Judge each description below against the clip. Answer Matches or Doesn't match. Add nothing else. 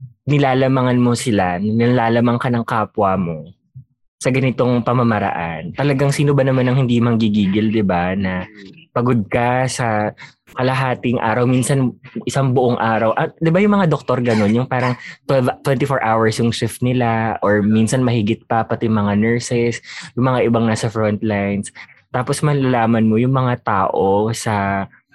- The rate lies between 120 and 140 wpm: Doesn't match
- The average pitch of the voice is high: Doesn't match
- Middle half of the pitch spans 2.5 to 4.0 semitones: Matches